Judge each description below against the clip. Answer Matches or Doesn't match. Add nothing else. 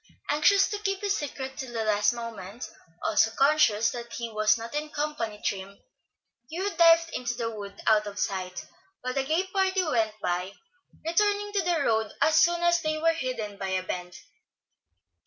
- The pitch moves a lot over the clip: Matches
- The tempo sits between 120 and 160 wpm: Doesn't match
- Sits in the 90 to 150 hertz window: Doesn't match